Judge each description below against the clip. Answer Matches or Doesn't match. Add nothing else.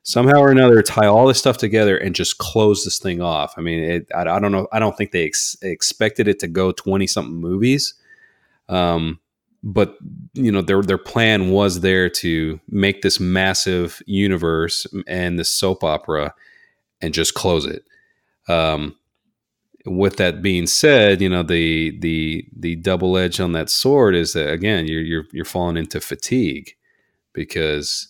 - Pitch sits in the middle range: Doesn't match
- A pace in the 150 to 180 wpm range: Matches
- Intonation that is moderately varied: Matches